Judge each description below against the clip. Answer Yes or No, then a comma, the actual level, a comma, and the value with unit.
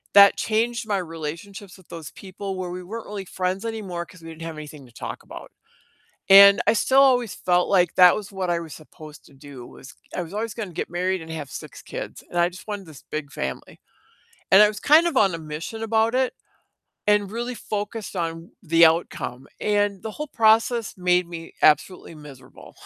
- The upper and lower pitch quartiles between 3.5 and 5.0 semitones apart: Yes, average, 4.4 semitones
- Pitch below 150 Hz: No, medium, 185 Hz